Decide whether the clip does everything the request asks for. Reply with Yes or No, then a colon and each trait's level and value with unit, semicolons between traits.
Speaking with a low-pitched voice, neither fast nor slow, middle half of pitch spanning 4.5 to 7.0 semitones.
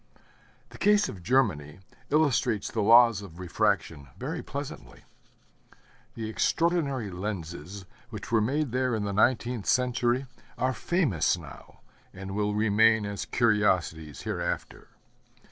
No: low, 110 Hz; slow, 120 wpm; average, 4.8 semitones